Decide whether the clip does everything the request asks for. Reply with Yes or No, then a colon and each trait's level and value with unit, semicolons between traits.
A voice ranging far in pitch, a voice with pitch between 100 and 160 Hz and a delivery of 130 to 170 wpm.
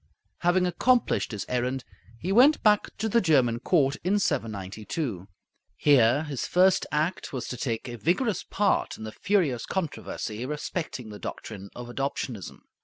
Yes: wide, 7.8 semitones; medium, 140 Hz; average, 150 wpm